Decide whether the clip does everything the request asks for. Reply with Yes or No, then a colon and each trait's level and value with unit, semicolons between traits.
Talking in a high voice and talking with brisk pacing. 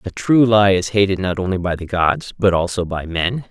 No: very low, 95 Hz; fast, 240 wpm